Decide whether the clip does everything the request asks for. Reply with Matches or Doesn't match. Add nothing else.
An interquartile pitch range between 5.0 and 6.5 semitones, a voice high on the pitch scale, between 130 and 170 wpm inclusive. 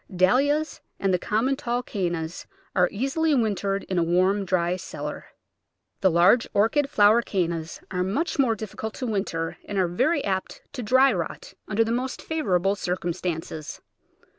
Matches